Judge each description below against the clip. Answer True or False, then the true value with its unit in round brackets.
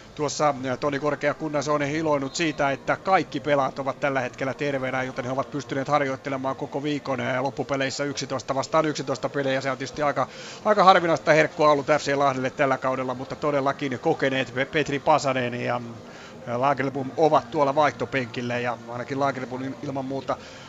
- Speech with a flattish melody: True (1.7 semitones)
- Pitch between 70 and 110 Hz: False (140 Hz)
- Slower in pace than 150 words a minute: False (155 wpm)